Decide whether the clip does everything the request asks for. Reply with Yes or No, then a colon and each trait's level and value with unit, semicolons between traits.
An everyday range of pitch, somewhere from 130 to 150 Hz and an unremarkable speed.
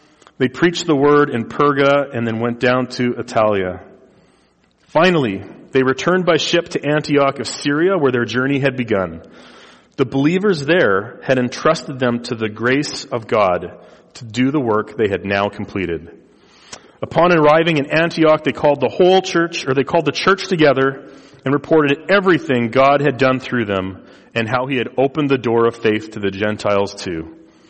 Yes: average, 4.5 semitones; low, 135 Hz; average, 175 wpm